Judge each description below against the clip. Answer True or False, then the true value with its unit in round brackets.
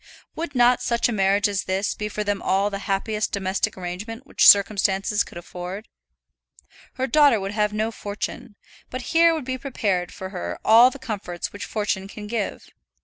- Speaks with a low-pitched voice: False (210 Hz)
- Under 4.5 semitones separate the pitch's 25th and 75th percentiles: True (3.4 semitones)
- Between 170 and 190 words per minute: True (180 wpm)